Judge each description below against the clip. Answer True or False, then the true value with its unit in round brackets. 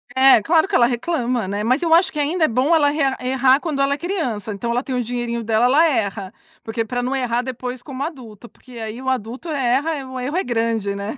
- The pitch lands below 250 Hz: False (255 Hz)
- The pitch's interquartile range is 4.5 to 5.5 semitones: False (3.8 semitones)